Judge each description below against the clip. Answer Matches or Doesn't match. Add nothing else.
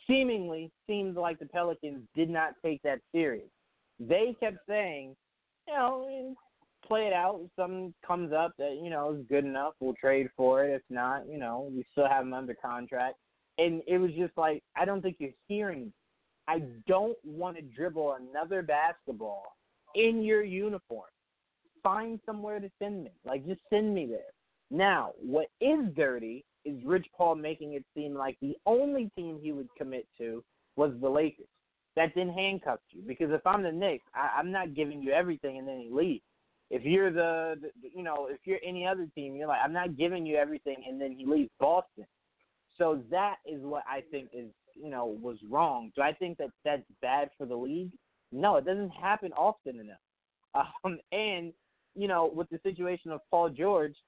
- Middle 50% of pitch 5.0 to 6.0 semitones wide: Matches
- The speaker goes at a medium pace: Matches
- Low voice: Doesn't match